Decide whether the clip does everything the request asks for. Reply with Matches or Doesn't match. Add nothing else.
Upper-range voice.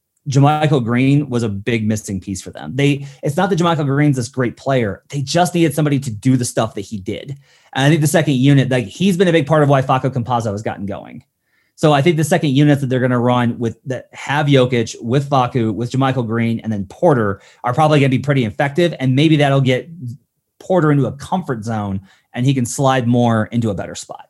Doesn't match